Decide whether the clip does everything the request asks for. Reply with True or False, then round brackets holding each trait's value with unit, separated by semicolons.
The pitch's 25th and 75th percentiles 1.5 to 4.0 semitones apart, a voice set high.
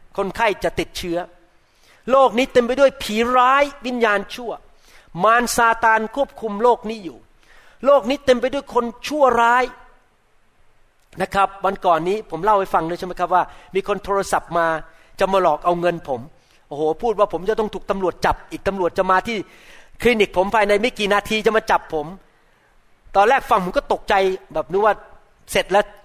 False (4.6 semitones; 205 Hz)